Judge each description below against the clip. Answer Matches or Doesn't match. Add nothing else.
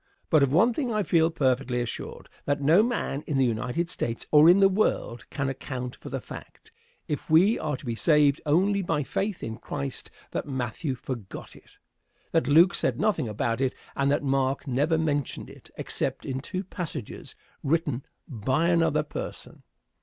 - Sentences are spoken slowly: Doesn't match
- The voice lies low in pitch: Doesn't match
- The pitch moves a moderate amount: Matches